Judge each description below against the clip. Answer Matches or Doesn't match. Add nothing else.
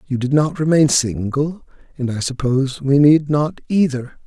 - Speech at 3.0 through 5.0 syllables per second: Matches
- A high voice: Doesn't match